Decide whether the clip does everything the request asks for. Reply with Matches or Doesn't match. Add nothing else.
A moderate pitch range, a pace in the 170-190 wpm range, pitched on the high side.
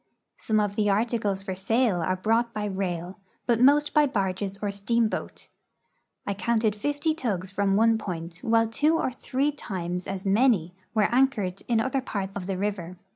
Matches